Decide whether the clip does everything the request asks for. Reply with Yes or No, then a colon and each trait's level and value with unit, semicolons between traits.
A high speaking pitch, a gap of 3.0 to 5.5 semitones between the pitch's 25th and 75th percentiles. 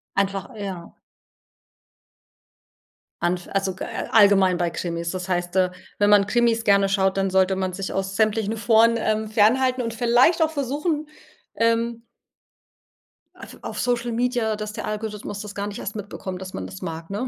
Yes: high, 205 Hz; average, 3.3 semitones